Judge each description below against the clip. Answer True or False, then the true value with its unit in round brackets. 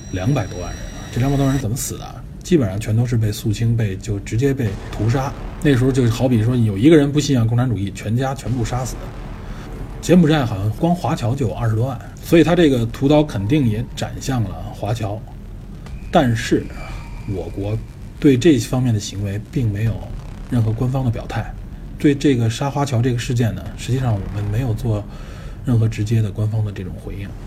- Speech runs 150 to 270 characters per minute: False (300 characters per minute)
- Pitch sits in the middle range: False (115 Hz)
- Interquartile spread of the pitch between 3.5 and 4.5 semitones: True (3.8 semitones)